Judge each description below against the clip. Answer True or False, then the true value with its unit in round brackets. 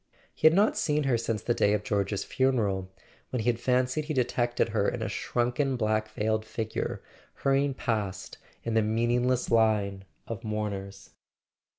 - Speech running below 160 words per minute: False (165 wpm)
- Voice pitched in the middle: False (115 Hz)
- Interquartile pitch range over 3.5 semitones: False (3.0 semitones)